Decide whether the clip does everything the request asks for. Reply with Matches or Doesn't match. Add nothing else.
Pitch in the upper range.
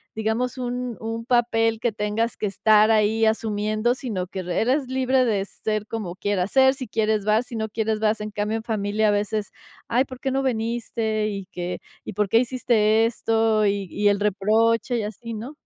Matches